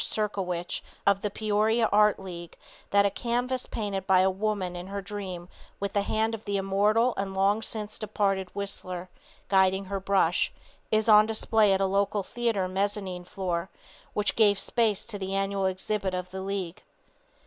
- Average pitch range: No, narrow, 1.9 semitones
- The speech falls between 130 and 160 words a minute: No, average, 170 wpm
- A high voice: Yes, high, 200 Hz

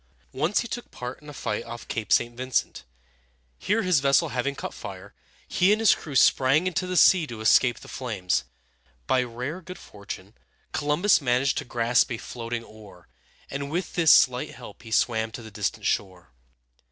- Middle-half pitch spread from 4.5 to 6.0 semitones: Yes, average, 5.1 semitones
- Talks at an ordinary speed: Yes, average, 180 wpm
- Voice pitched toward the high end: No, low, 125 Hz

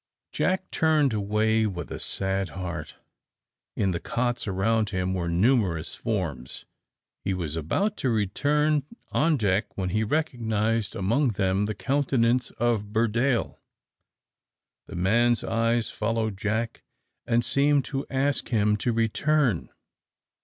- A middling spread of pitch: Yes, average, 4.5 semitones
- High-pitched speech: No, low, 110 Hz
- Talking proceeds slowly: Yes, slow, 125 wpm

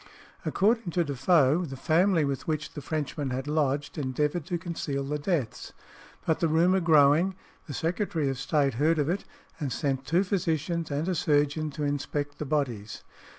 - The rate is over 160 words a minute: Yes, average, 170 wpm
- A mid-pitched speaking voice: Yes, medium, 150 Hz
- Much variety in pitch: No, average, 3.0 semitones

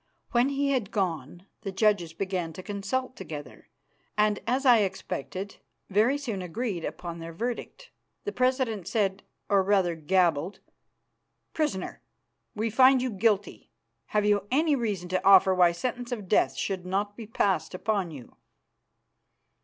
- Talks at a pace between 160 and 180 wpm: No, average, 145 wpm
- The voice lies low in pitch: No, high, 200 Hz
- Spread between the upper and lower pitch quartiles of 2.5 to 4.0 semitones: No, average, 4.6 semitones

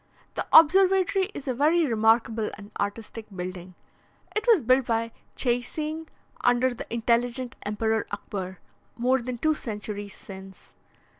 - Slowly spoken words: Yes, slow, 130 wpm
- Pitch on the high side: Yes, high, 235 Hz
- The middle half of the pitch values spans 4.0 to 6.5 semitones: Yes, average, 4.7 semitones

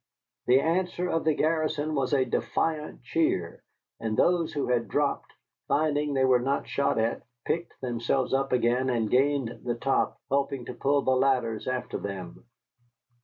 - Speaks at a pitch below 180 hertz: Yes, low, 135 Hz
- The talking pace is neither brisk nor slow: Yes, average, 160 wpm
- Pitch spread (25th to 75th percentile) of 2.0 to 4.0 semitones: Yes, average, 3.3 semitones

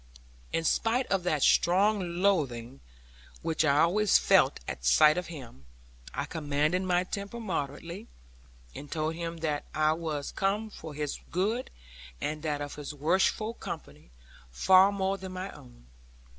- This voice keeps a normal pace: Yes, average, 150 wpm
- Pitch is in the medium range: Yes, medium, 165 Hz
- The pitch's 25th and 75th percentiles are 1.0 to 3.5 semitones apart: No, average, 4.6 semitones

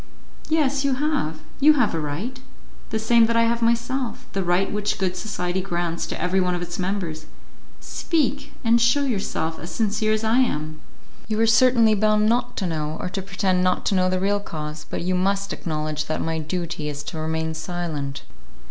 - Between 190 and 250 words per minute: Yes, average, 195 wpm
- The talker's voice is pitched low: No, high, 190 Hz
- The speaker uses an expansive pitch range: Yes, wide, 5.7 semitones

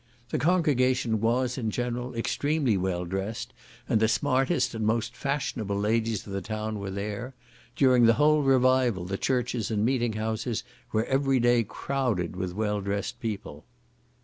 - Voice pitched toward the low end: Yes, low, 115 Hz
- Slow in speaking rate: No, average, 155 wpm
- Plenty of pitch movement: No, average, 3.7 semitones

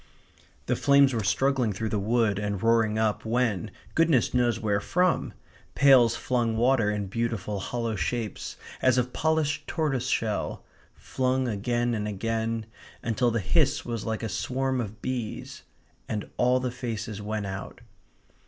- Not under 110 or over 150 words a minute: Yes, average, 145 wpm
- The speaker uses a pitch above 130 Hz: No, low, 115 Hz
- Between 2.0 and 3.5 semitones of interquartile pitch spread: Yes, average, 3.1 semitones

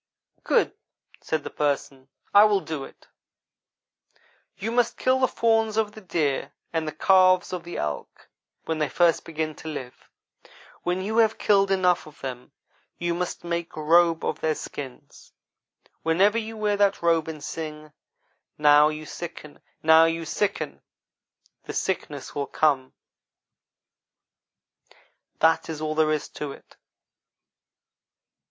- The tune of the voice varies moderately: Yes, average, 4.1 semitones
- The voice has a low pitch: No, medium, 165 Hz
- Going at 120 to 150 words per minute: Yes, average, 140 wpm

